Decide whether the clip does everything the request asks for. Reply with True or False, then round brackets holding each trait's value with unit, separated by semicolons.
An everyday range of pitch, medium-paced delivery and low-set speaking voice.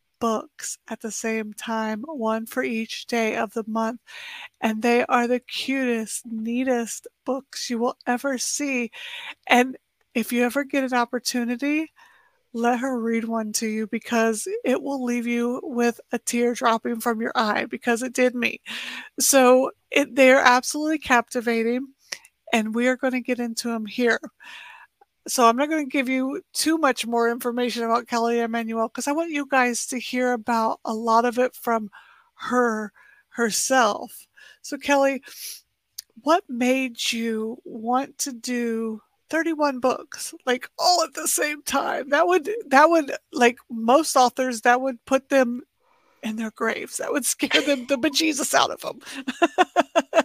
False (3.2 semitones; 160 wpm; 250 Hz)